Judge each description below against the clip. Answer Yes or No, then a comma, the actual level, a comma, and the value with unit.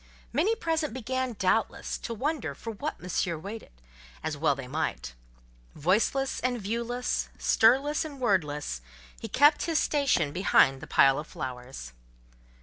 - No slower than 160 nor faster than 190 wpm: No, average, 140 wpm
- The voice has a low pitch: No, high, 225 Hz